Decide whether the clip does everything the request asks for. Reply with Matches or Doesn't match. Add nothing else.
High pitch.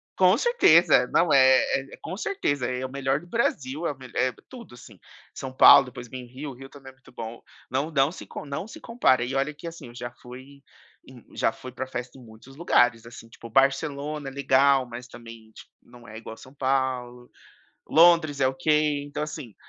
Doesn't match